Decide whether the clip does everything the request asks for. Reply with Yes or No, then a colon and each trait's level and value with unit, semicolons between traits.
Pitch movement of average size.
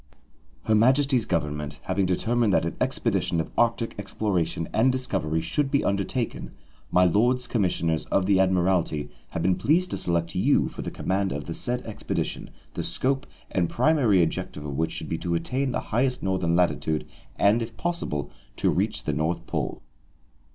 No: wide, 6.5 semitones